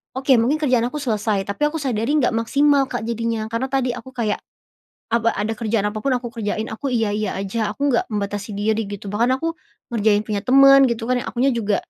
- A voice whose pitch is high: Yes, high, 230 Hz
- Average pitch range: Yes, average, 3.6 semitones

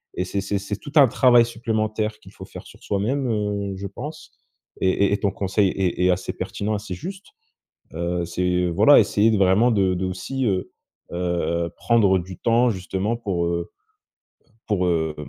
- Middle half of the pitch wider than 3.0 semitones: Yes, average, 3.6 semitones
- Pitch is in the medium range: No, low, 100 Hz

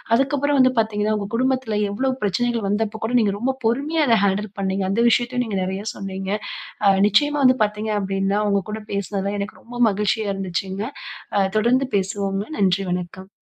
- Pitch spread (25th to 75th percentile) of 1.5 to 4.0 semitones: Yes, average, 3.6 semitones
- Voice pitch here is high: Yes, high, 210 Hz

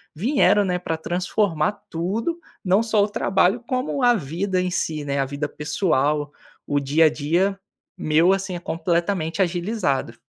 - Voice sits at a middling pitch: Yes, medium, 175 Hz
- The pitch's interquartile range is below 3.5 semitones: No, average, 4.5 semitones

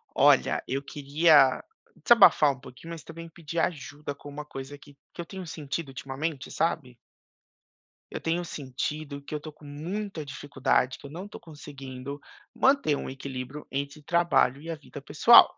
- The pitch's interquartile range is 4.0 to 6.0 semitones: No, average, 3.1 semitones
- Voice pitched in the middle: Yes, medium, 145 Hz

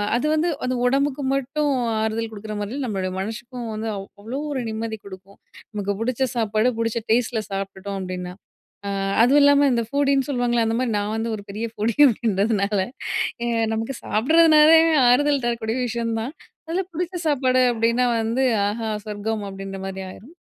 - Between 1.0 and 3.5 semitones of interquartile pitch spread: No, average, 3.9 semitones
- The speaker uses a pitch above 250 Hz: No, high, 230 Hz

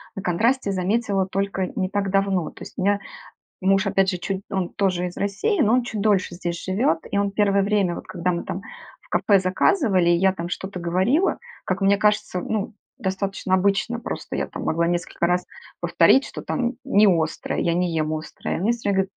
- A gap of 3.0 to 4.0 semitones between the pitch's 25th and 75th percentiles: No, narrow, 2.4 semitones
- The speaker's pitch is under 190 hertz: No, high, 195 Hz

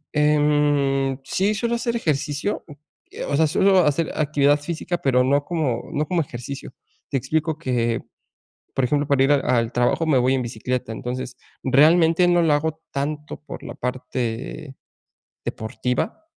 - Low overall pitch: No, medium, 145 Hz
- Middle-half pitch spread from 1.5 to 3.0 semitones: No, average, 3.7 semitones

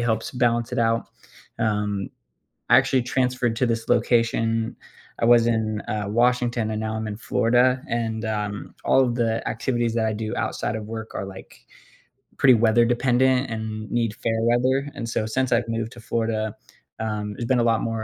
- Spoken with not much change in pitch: Yes, narrow, 1.6 semitones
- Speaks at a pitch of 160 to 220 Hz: No, low, 115 Hz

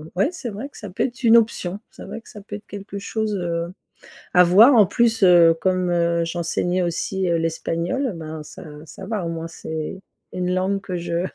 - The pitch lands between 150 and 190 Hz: Yes, medium, 185 Hz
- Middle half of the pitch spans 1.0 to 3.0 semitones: No, average, 3.6 semitones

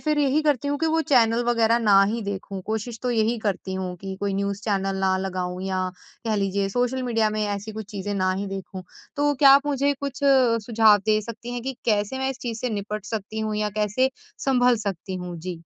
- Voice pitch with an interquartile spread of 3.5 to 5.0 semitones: Yes, average, 4.0 semitones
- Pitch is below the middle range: No, high, 215 Hz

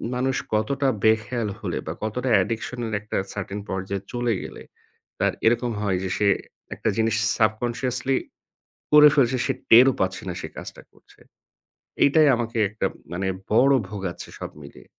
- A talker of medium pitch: No, low, 115 Hz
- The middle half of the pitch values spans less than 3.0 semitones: No, average, 3.5 semitones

